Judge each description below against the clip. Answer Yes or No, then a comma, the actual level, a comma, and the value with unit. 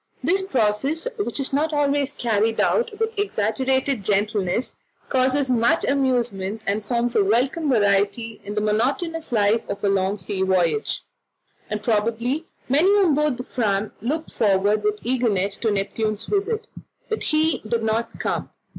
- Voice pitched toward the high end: Yes, high, 235 Hz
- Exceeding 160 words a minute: No, average, 150 wpm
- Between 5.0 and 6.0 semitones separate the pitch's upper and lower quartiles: Yes, wide, 5.4 semitones